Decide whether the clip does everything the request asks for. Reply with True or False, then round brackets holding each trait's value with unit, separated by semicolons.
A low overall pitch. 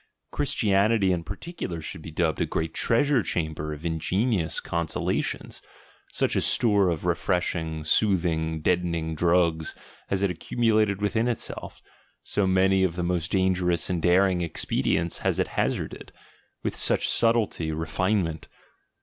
True (90 Hz)